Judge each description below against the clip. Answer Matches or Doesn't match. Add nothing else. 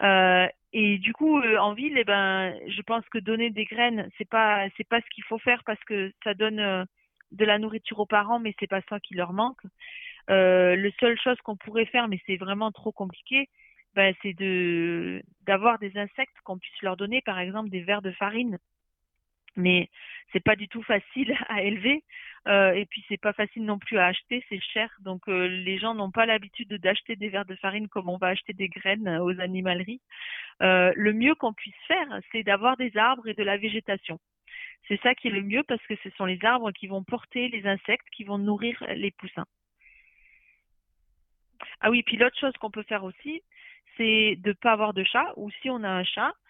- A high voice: Matches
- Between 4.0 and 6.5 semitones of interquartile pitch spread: Doesn't match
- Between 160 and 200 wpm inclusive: Doesn't match